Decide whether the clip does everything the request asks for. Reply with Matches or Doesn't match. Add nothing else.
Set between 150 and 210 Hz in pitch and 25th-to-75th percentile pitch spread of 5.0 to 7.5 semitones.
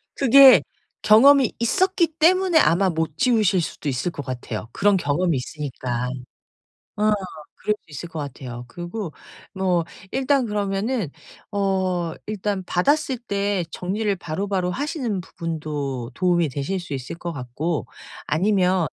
Matches